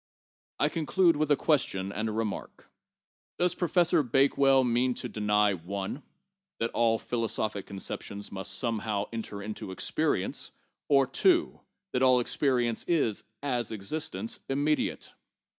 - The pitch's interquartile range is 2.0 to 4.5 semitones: No, wide, 5.4 semitones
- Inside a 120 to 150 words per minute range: Yes, slow, 135 wpm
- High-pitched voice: No, low, 120 Hz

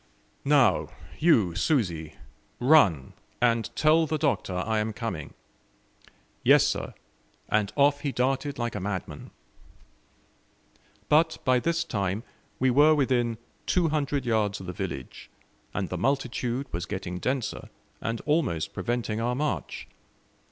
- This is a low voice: Yes, low, 120 Hz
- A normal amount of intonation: No, wide, 5.8 semitones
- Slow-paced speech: Yes, slow, 130 wpm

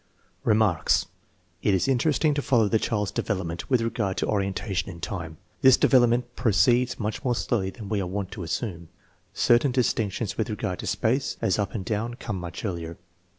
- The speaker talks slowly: No, average, 190 wpm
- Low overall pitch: Yes, low, 105 Hz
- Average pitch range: Yes, average, 4.1 semitones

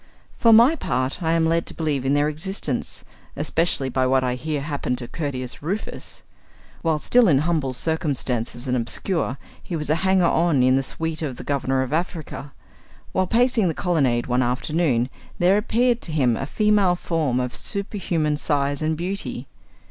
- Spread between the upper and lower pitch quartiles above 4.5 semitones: Yes, average, 4.9 semitones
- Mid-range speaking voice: Yes, medium, 155 Hz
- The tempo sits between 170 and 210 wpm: Yes, average, 175 wpm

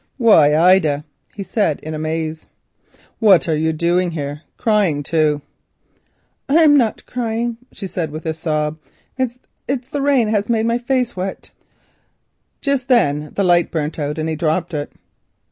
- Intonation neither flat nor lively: No, wide, 6.9 semitones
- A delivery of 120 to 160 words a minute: Yes, average, 155 wpm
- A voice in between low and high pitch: Yes, medium, 175 Hz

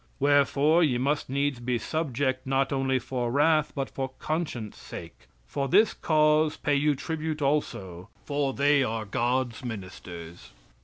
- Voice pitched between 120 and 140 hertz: Yes, low, 135 Hz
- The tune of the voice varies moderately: Yes, average, 3.5 semitones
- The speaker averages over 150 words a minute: No, average, 145 wpm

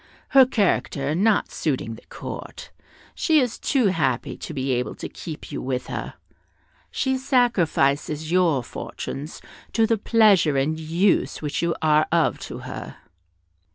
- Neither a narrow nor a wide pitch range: No, wide, 7.6 semitones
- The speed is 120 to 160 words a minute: Yes, average, 145 wpm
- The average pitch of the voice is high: No, medium, 160 Hz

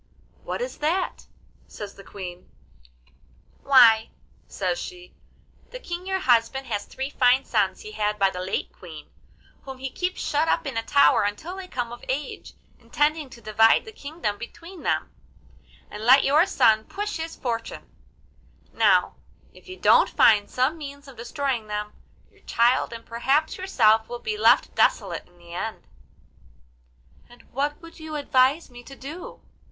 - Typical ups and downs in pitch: No, wide, 6.1 semitones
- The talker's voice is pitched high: Yes, very high, 260 Hz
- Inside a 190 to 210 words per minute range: No, average, 160 wpm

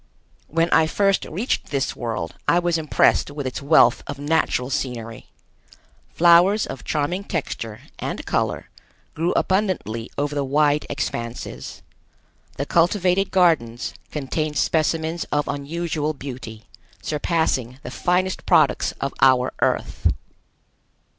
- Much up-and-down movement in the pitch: No, average, 4.7 semitones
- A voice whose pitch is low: No, medium, 150 Hz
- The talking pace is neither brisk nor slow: No, slow, 120 wpm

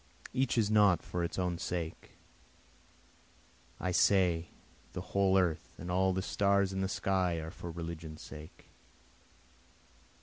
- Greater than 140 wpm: No, slow, 135 wpm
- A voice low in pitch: Yes, very low, 90 Hz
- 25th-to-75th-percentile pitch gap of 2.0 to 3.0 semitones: Yes, narrow, 2.4 semitones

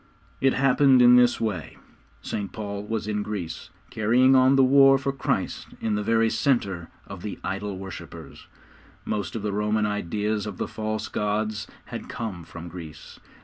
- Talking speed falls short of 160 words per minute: No, average, 165 wpm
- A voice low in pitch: Yes, low, 105 Hz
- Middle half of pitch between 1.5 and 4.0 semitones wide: Yes, average, 3.3 semitones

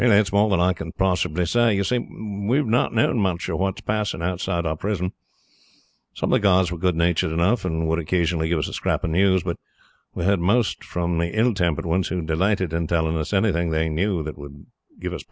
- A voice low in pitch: Yes, very low, 90 Hz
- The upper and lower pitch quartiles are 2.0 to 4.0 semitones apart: Yes, average, 3.4 semitones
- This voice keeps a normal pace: No, fast, 235 wpm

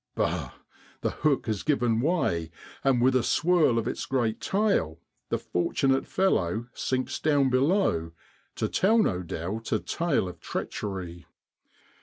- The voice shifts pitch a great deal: Yes, wide, 8.4 semitones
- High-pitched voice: No, low, 125 Hz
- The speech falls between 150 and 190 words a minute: No, average, 140 wpm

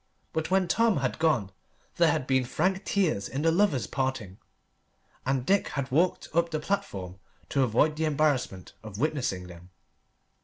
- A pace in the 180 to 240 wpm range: No, average, 160 wpm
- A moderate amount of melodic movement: No, wide, 5.9 semitones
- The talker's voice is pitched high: No, medium, 140 Hz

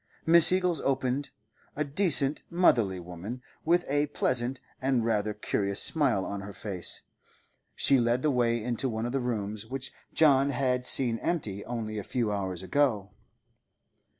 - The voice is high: No, low, 125 Hz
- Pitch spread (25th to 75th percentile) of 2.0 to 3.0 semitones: No, average, 4.8 semitones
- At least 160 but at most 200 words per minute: No, average, 150 wpm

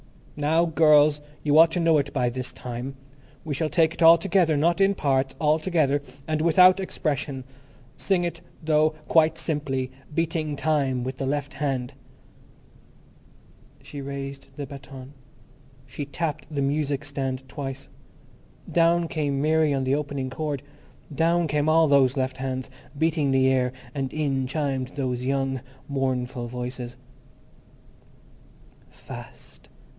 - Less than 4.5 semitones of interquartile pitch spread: Yes, average, 2.9 semitones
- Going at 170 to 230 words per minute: No, average, 140 wpm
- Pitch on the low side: No, medium, 145 Hz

